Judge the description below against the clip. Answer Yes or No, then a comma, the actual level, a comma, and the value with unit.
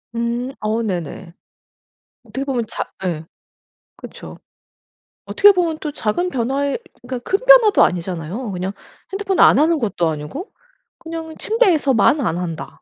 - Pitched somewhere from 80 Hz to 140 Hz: No, very high, 250 Hz